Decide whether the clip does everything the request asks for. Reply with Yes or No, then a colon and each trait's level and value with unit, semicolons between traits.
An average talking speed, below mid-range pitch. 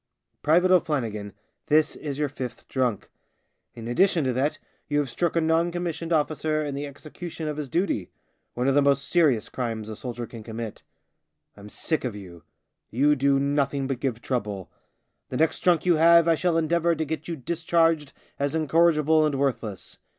No: average, 180 wpm; medium, 145 Hz